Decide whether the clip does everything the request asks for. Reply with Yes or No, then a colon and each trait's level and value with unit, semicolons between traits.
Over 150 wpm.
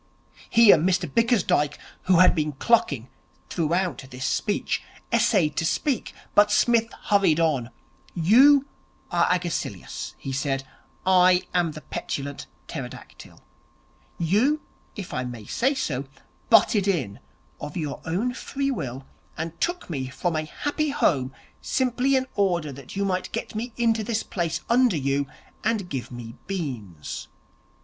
No: average, 140 wpm